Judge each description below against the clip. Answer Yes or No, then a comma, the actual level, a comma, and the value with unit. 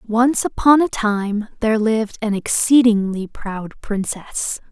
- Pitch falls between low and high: No, high, 220 Hz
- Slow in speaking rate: Yes, slow, 125 wpm